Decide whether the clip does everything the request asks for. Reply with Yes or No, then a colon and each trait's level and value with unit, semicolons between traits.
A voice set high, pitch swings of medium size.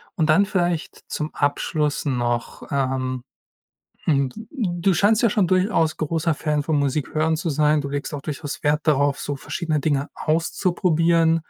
No: medium, 155 Hz; average, 3.2 semitones